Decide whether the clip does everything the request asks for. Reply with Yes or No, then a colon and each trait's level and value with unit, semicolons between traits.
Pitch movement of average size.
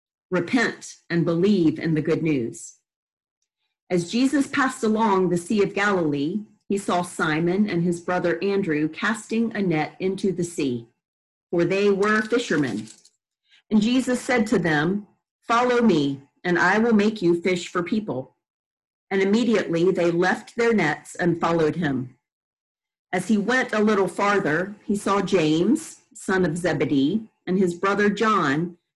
Yes: average, 4.1 semitones